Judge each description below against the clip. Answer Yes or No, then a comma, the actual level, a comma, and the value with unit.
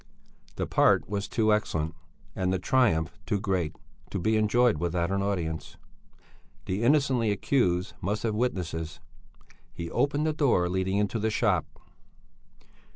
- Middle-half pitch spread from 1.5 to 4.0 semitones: No, average, 4.4 semitones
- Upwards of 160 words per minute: No, average, 140 wpm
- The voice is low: Yes, low, 100 Hz